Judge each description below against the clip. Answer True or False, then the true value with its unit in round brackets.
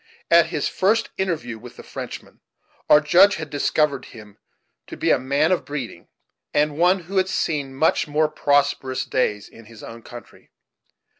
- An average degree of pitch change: True (5.0 semitones)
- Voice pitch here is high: False (145 Hz)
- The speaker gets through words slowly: False (165 wpm)